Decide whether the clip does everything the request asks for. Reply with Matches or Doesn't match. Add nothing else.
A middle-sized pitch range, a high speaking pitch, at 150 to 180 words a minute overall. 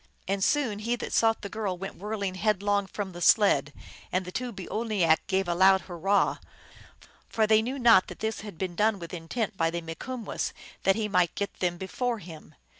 Doesn't match